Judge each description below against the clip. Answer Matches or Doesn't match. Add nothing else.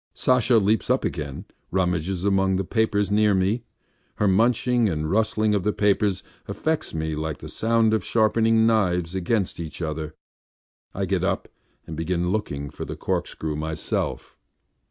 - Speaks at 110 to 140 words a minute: Doesn't match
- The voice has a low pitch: Matches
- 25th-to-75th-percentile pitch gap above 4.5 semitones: Matches